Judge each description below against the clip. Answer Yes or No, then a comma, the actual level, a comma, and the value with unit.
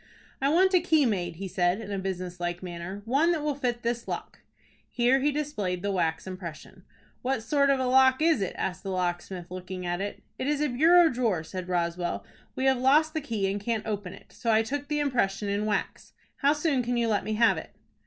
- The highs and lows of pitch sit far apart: Yes, wide, 6.9 semitones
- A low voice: No, high, 220 Hz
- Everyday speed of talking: No, fast, 225 wpm